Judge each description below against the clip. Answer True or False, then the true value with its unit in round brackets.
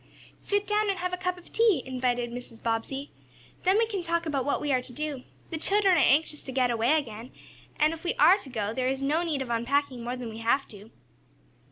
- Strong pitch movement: True (5.9 semitones)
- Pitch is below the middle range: False (280 Hz)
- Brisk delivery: True (235 wpm)